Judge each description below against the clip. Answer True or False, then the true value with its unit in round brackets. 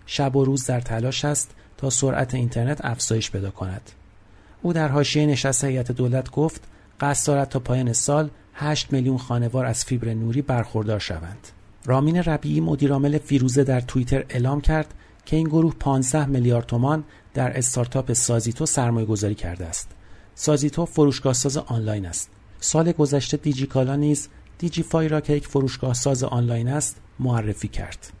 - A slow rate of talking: False (155 wpm)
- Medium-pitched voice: False (130 Hz)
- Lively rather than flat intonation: False (4.5 semitones)